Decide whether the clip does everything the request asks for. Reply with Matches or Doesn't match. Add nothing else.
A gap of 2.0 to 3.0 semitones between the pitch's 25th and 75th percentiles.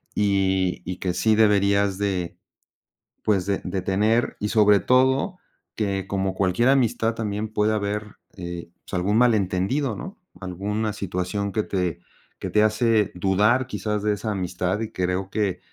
Matches